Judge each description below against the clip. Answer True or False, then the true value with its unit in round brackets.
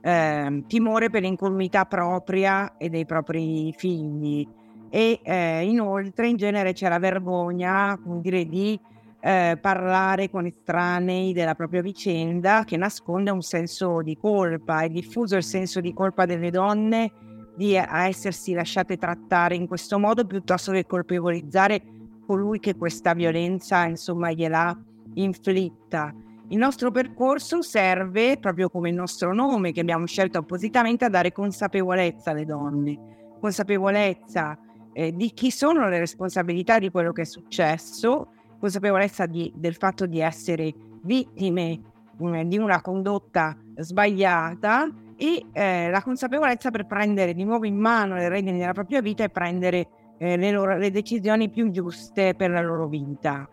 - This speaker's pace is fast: False (145 wpm)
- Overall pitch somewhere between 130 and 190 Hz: True (185 Hz)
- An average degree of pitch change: True (3.1 semitones)